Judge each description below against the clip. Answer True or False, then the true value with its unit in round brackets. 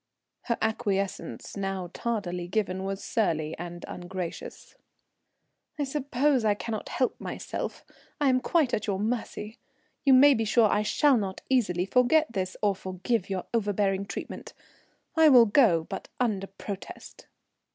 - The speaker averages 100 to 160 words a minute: True (140 wpm)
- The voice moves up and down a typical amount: True (4.6 semitones)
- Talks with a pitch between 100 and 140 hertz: False (210 Hz)